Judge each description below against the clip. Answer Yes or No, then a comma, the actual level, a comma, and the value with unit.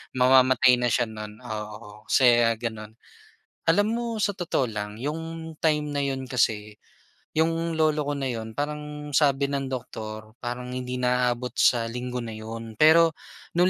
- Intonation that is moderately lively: Yes, average, 4.7 semitones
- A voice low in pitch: Yes, low, 125 Hz